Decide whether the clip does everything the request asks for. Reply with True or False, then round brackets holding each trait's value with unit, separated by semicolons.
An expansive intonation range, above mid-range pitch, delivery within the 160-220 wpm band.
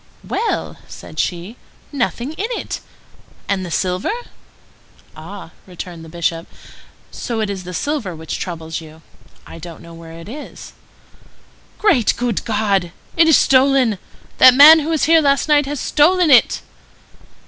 False (9.0 semitones; 215 Hz; 150 wpm)